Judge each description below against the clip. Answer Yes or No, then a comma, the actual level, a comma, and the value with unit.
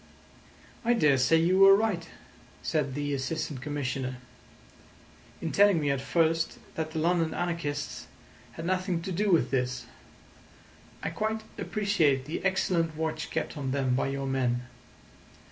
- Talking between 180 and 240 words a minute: No, average, 140 wpm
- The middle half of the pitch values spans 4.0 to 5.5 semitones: Yes, average, 4.5 semitones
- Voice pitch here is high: No, medium, 160 Hz